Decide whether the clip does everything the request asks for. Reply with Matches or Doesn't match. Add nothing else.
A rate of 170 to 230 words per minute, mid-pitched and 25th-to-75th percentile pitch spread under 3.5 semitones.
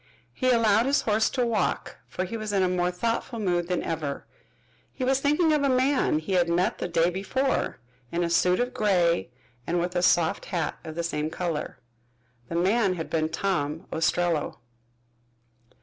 Doesn't match